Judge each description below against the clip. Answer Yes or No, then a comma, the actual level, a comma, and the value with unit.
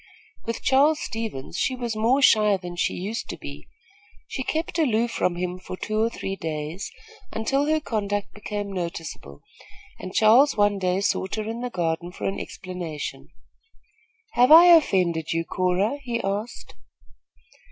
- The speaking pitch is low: No, high, 205 Hz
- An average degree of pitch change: Yes, average, 4.9 semitones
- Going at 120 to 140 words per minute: No, average, 155 wpm